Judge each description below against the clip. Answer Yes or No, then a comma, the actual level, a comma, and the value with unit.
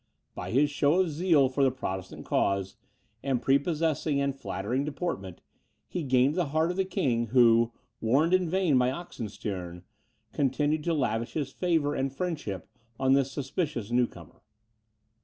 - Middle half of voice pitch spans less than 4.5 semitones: No, average, 4.9 semitones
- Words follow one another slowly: No, average, 155 wpm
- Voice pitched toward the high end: No, low, 135 Hz